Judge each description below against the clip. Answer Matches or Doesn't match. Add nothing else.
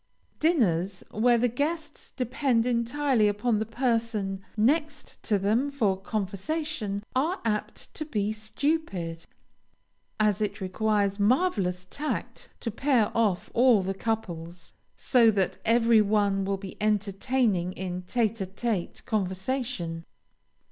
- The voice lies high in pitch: Matches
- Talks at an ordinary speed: Doesn't match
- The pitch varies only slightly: Doesn't match